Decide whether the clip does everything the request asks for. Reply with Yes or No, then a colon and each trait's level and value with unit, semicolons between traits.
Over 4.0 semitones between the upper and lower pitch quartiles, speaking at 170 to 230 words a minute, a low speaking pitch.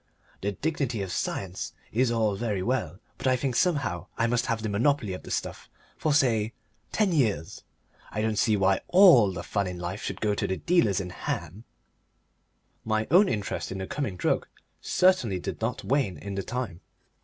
Yes: average, 5.1 semitones; average, 190 wpm; low, 110 Hz